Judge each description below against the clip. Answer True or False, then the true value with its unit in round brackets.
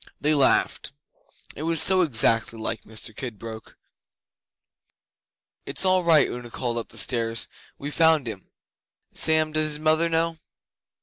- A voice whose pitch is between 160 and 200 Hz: False (145 Hz)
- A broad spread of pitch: True (5.8 semitones)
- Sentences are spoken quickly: False (135 wpm)